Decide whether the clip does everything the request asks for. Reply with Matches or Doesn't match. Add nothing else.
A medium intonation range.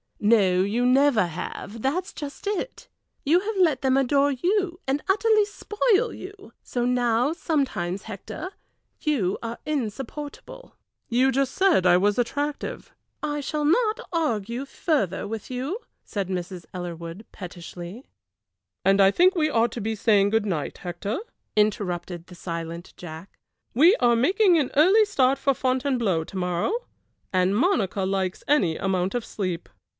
Doesn't match